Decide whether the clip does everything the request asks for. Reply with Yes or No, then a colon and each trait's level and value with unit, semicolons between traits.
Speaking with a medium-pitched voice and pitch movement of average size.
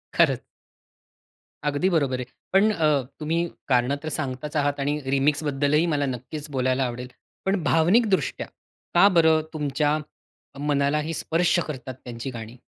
Yes: medium, 145 Hz; average, 3.2 semitones